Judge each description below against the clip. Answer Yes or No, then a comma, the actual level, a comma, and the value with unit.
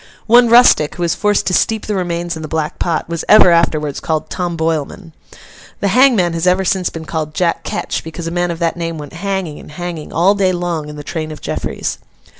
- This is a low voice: No, medium, 170 Hz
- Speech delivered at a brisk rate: Yes, fast, 225 wpm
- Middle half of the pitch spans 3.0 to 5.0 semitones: No, narrow, 2.6 semitones